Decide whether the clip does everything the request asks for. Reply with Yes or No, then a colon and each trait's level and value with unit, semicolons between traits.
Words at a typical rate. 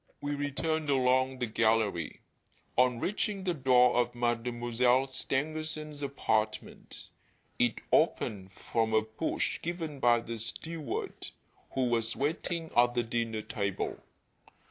No: slow, 120 wpm